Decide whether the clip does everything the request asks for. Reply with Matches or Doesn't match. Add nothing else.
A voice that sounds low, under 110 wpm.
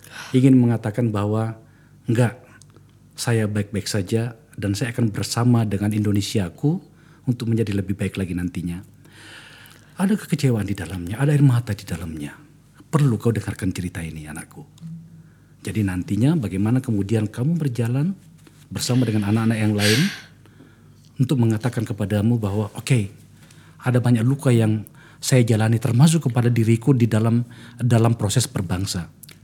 Doesn't match